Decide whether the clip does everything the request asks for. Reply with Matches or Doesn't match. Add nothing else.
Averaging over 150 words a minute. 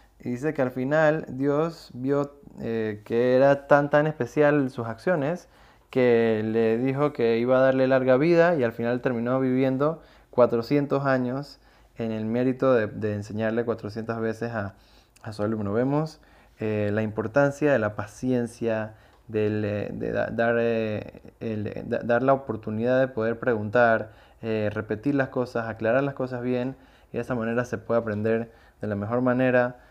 Matches